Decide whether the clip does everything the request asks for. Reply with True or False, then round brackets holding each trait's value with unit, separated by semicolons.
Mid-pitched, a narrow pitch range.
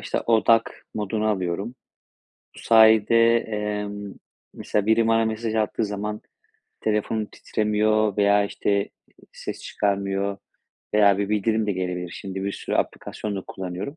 False (105 Hz; 1.7 semitones)